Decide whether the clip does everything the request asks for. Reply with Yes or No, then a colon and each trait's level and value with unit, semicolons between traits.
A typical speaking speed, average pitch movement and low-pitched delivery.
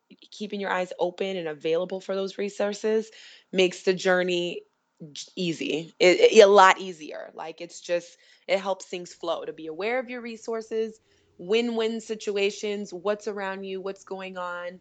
No: average, 160 wpm; average, 3.1 semitones; high, 190 Hz